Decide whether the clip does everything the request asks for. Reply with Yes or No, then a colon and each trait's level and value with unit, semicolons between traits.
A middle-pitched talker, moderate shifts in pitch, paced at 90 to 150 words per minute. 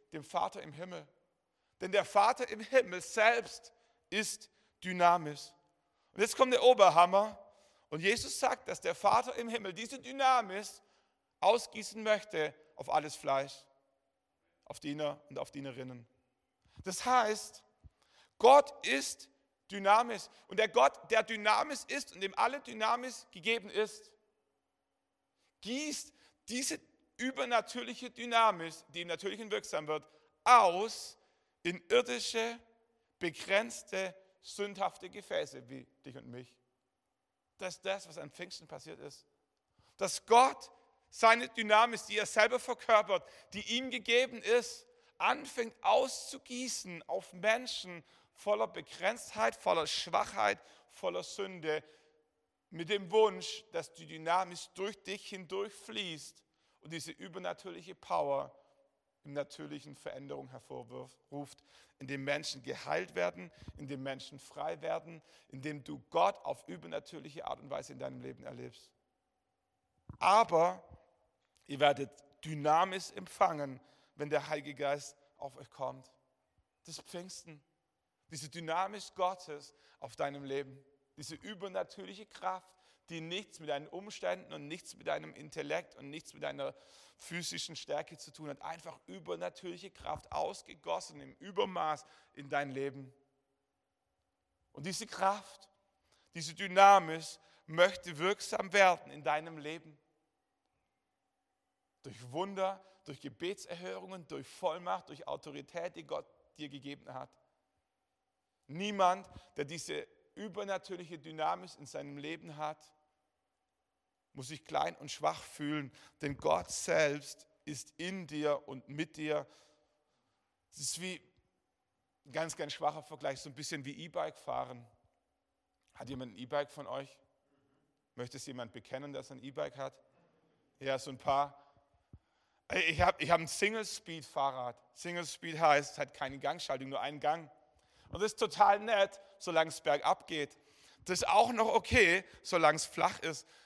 No: medium, 170 Hz; wide, 6.8 semitones; slow, 125 wpm